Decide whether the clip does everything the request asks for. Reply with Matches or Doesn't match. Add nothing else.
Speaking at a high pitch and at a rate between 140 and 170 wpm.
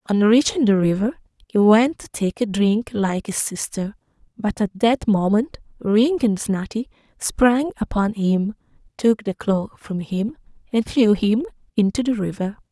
Matches